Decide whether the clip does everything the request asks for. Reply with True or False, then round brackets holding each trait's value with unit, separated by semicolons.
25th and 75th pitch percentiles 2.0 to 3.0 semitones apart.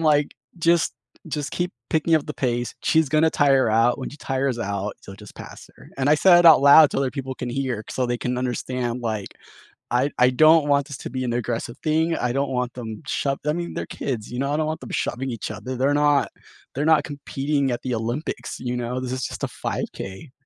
False (3.4 semitones)